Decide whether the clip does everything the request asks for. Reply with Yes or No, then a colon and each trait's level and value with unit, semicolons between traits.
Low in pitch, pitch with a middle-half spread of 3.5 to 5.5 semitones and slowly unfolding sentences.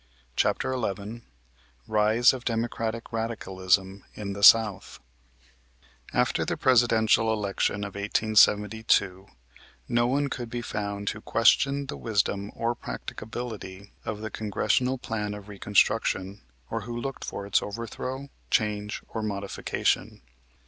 No: low, 110 Hz; narrow, 2.6 semitones; slow, 120 wpm